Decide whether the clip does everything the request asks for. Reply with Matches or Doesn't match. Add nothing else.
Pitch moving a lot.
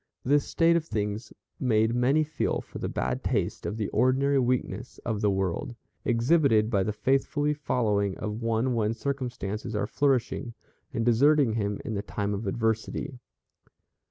Doesn't match